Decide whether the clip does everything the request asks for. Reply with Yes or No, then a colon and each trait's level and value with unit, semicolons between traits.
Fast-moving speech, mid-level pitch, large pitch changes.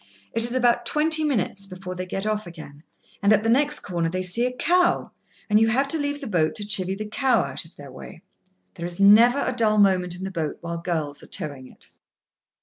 No: fast, 230 wpm; high, 200 Hz; wide, 5.7 semitones